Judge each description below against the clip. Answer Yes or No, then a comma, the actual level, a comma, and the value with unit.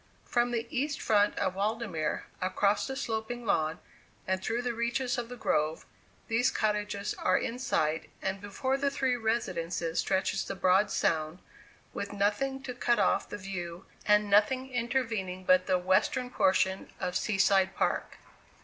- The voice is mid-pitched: No, high, 205 Hz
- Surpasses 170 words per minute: No, average, 160 wpm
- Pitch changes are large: No, average, 4.4 semitones